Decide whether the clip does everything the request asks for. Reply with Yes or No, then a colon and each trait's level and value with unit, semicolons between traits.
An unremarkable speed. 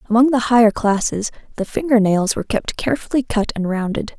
Yes: average, 185 wpm